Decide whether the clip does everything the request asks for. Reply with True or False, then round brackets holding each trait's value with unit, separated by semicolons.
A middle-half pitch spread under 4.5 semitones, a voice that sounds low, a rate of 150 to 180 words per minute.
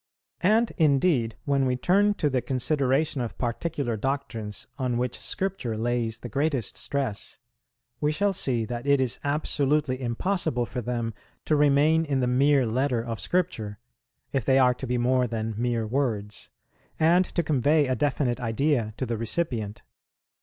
True (3.9 semitones; 130 Hz; 160 wpm)